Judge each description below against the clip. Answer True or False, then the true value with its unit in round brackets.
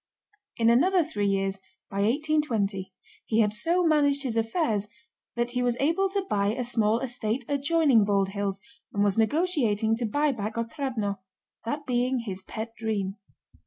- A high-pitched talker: True (230 Hz)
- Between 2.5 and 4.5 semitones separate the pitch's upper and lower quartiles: False (5.6 semitones)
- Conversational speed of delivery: True (155 wpm)